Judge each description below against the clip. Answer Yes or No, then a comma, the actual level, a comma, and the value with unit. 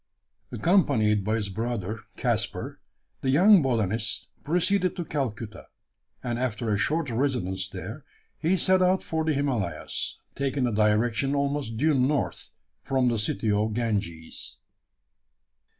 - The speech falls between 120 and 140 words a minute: Yes, slow, 135 wpm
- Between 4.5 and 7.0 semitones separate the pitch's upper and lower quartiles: Yes, average, 5.3 semitones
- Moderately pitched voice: No, low, 120 Hz